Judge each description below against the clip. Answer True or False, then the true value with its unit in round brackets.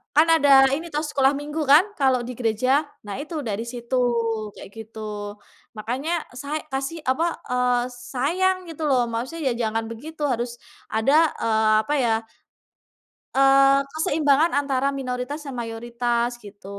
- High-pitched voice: True (265 Hz)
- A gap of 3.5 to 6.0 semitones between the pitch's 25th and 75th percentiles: True (3.8 semitones)